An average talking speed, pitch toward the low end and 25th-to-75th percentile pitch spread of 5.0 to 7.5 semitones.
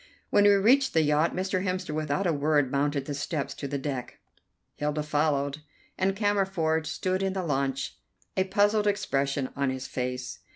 No: average, 170 wpm; medium, 155 Hz; average, 5.3 semitones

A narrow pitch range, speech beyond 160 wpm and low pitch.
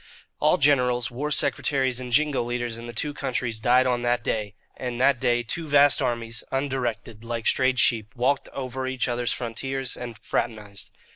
Yes: narrow, 2.0 semitones; average, 170 wpm; low, 125 Hz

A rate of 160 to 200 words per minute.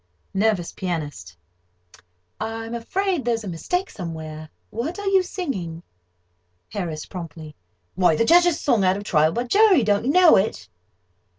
No: average, 140 wpm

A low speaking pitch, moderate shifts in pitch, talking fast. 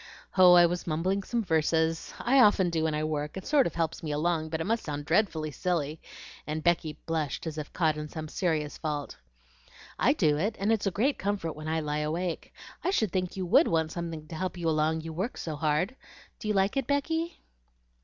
No: medium, 165 Hz; average, 3.7 semitones; fast, 220 wpm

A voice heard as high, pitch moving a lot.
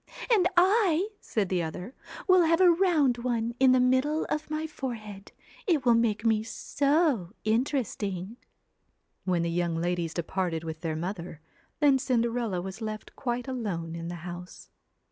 Yes: high, 230 Hz; wide, 7.8 semitones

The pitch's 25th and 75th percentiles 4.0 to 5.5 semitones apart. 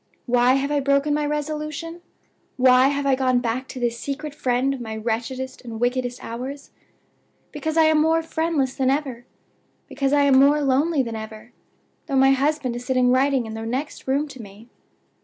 No: average, 2.9 semitones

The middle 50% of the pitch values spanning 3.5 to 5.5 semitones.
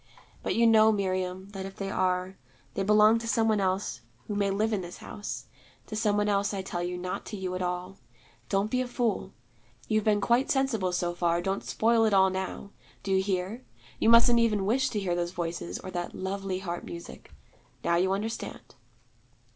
No: average, 2.9 semitones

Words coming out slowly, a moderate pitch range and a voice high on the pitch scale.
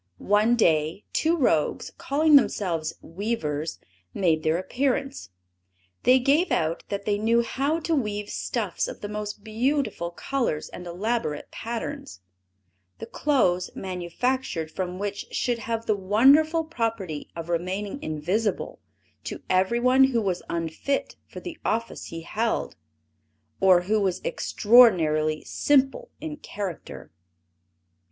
No: slow, 125 wpm; wide, 6.4 semitones; high, 210 Hz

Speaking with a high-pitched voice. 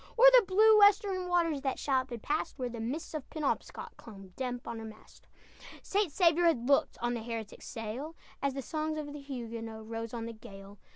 Yes: very high, 265 Hz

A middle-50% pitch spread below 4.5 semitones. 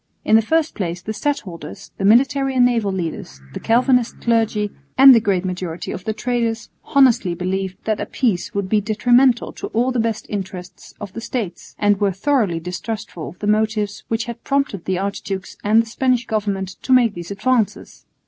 Yes: average, 4.0 semitones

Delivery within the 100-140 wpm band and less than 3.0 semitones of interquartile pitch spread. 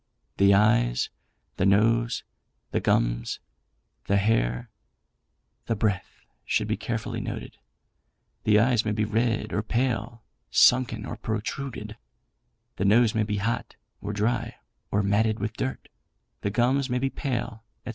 Yes: slow, 135 wpm; narrow, 2.5 semitones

